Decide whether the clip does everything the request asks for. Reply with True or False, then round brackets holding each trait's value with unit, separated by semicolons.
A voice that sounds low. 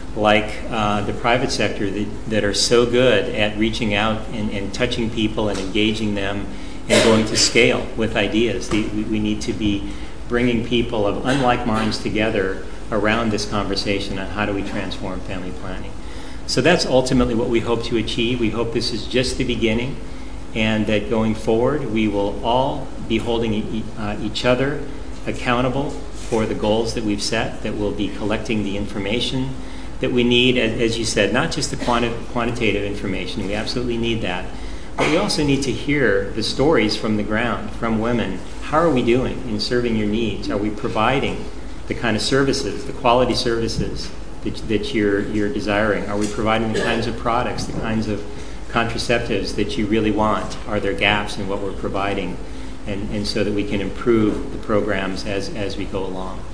True (110 Hz)